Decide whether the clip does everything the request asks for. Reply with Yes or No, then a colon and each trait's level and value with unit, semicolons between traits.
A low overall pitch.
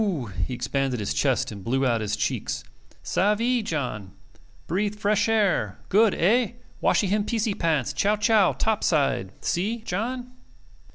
No: high, 195 Hz